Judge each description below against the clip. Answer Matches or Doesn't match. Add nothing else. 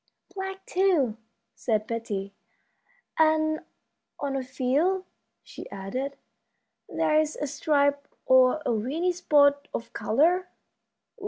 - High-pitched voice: Matches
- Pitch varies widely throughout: Doesn't match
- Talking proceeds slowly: Matches